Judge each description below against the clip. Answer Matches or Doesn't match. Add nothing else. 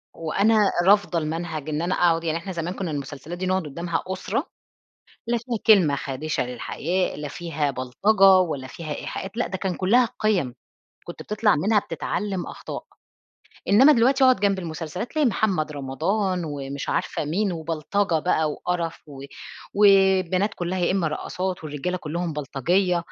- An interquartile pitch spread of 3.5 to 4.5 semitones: Matches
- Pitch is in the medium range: Matches